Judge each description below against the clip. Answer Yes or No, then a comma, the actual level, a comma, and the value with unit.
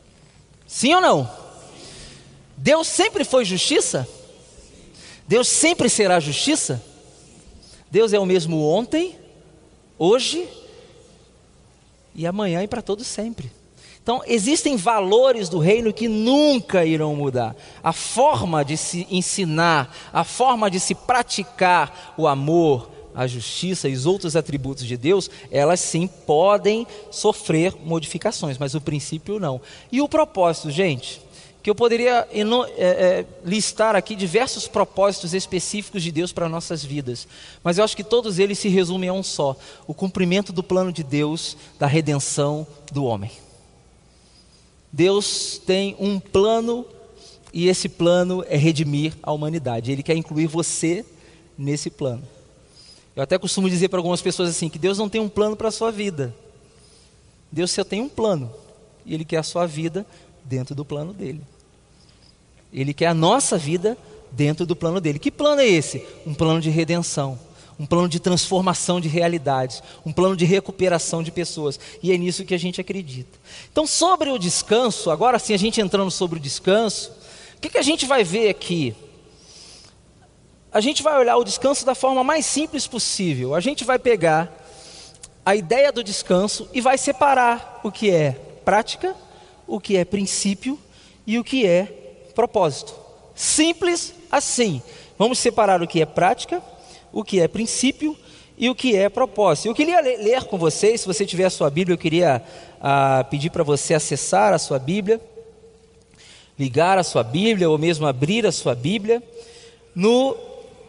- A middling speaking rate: Yes, average, 160 wpm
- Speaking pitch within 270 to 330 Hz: No, medium, 185 Hz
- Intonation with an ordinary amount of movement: No, wide, 5.9 semitones